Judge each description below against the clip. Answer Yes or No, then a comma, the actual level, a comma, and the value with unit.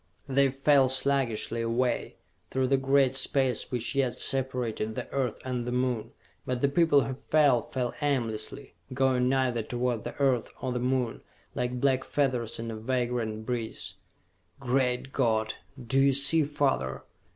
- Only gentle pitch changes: Yes, narrow, 2.2 semitones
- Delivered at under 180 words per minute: Yes, average, 150 wpm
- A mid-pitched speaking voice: No, low, 125 Hz